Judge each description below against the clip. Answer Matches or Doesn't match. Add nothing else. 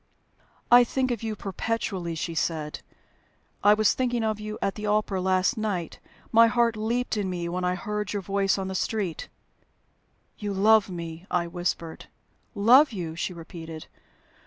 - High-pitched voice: Matches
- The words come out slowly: Doesn't match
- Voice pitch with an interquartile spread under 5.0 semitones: Matches